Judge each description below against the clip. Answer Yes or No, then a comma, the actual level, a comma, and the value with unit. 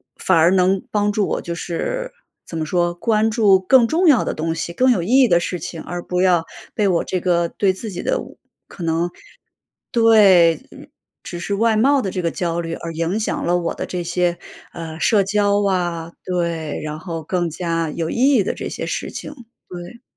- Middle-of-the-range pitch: Yes, medium, 180 Hz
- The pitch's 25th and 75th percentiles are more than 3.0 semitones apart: Yes, average, 3.7 semitones